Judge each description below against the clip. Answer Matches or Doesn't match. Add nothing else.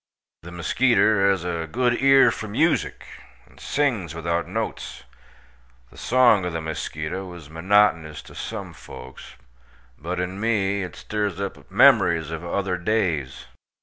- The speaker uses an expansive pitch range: Doesn't match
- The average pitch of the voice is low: Matches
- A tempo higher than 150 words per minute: Doesn't match